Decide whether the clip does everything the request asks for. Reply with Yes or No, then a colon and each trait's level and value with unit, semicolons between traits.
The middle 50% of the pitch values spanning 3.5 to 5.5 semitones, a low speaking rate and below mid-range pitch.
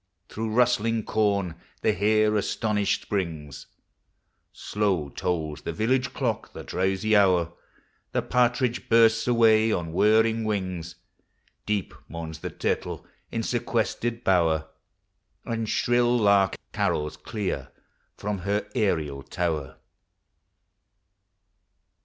Yes: average, 4.3 semitones; slow, 105 wpm; low, 105 Hz